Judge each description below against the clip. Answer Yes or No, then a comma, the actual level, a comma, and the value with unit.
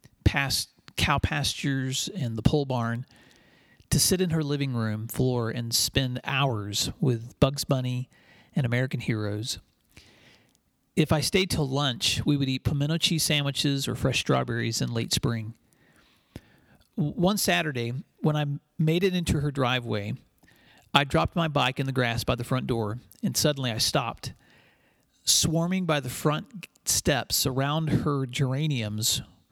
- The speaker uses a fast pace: No, average, 145 wpm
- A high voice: No, low, 135 Hz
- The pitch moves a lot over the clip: No, average, 4.3 semitones